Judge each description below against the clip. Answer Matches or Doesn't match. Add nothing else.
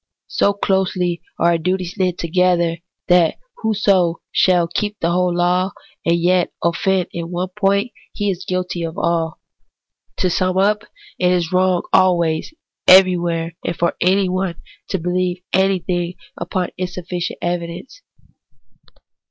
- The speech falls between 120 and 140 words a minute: Matches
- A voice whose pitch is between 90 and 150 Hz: Doesn't match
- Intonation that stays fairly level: Matches